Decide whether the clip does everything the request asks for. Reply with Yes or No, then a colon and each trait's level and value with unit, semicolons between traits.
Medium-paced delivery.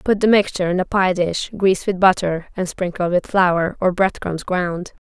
No: fast, 215 wpm